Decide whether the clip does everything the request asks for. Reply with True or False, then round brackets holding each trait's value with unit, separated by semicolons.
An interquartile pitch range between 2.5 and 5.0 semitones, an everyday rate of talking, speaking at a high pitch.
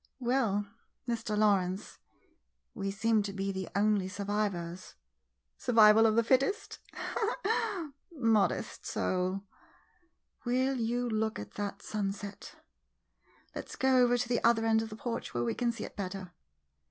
True (3.4 semitones; 150 wpm; 215 Hz)